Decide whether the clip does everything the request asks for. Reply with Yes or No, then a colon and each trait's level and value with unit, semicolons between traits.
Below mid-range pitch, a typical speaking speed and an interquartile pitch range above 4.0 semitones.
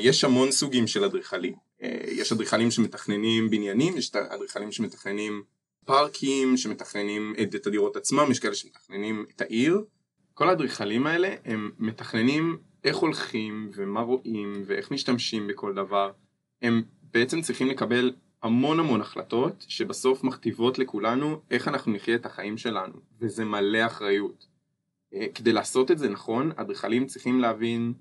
No: low, 115 Hz; average, 135 wpm; average, 3.5 semitones